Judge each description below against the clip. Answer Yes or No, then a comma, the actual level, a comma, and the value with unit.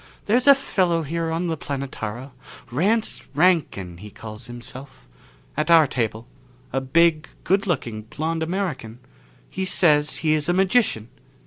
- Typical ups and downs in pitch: No, wide, 5.9 semitones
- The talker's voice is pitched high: No, medium, 155 Hz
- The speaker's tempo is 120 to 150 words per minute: Yes, average, 140 wpm